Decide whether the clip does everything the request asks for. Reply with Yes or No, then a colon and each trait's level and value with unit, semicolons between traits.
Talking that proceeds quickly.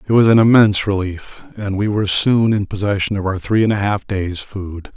Yes: fast, 230 wpm